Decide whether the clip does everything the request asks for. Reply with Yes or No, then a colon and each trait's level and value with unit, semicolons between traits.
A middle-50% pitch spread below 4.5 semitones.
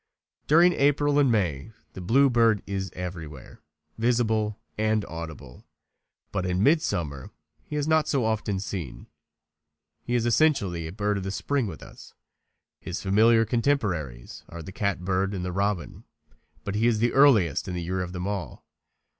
No: average, 4.9 semitones